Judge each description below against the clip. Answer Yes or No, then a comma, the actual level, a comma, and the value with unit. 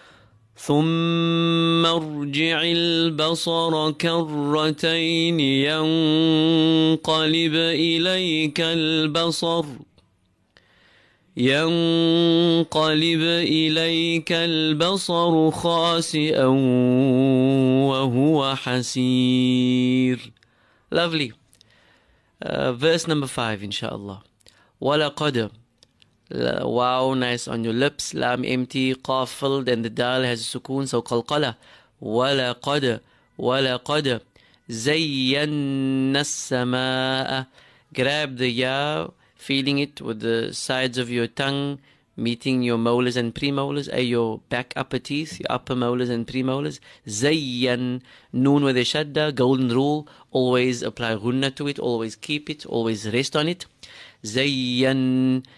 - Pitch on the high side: No, low, 135 Hz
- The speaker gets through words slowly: Yes, slow, 100 wpm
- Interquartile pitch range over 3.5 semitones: Yes, average, 4.0 semitones